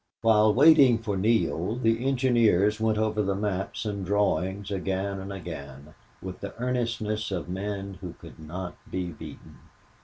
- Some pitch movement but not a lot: Yes, average, 3.0 semitones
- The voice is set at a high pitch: No, low, 100 Hz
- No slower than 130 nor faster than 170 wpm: Yes, average, 150 wpm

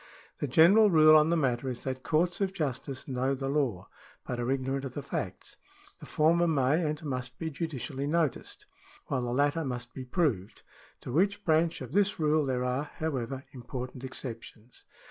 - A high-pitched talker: No, medium, 140 Hz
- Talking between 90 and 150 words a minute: No, average, 180 wpm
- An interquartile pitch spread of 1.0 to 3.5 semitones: No, average, 3.9 semitones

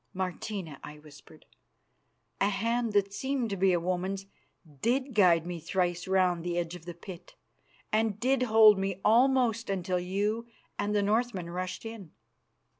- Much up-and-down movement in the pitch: No, average, 4.0 semitones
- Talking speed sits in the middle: Yes, average, 155 wpm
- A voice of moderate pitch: No, high, 195 Hz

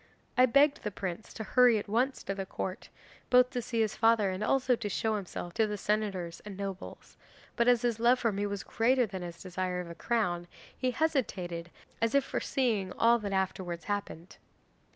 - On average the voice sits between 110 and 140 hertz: No, high, 210 Hz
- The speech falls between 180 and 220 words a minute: Yes, average, 195 wpm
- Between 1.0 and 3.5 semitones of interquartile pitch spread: No, average, 4.2 semitones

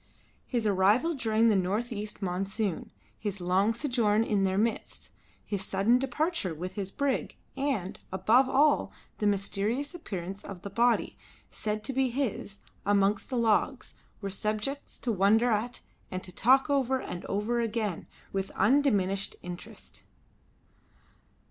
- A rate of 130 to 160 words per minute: Yes, average, 140 wpm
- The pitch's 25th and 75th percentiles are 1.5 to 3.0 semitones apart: No, average, 3.9 semitones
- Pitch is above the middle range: Yes, high, 215 Hz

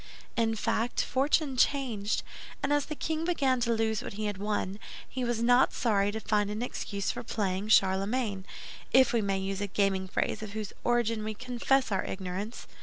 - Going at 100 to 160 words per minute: No, average, 180 wpm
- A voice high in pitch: Yes, high, 220 Hz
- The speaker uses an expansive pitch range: No, average, 3.7 semitones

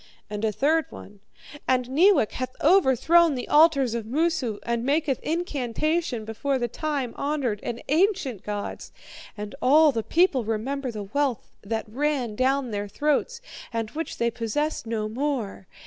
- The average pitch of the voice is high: Yes, very high, 260 Hz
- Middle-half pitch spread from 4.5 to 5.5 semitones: Yes, average, 5.2 semitones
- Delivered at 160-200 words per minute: No, average, 150 wpm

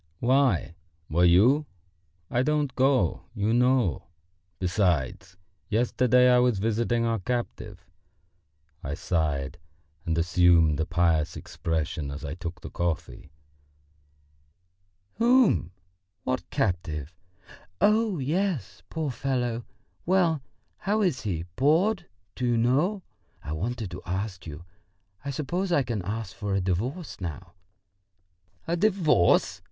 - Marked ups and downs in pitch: Yes, wide, 7.8 semitones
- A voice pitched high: No, low, 115 Hz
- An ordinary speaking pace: No, slow, 115 wpm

